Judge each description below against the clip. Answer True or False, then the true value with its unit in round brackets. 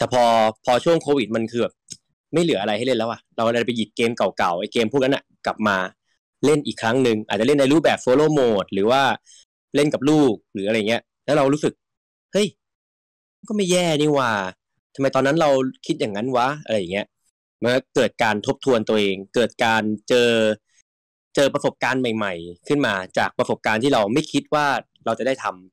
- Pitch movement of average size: True (4.9 semitones)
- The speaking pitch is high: False (120 Hz)